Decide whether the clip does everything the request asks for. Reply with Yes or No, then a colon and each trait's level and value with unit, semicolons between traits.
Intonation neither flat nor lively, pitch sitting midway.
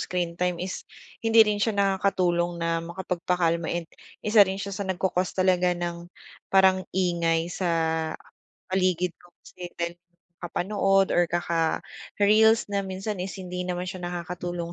No: narrow, 1.9 semitones; medium, 180 Hz